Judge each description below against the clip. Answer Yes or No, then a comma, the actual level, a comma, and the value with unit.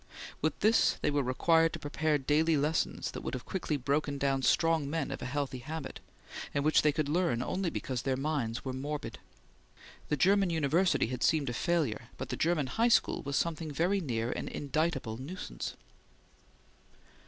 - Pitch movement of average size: Yes, average, 3.6 semitones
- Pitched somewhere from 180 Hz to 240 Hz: No, medium, 150 Hz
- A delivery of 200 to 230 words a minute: No, average, 175 wpm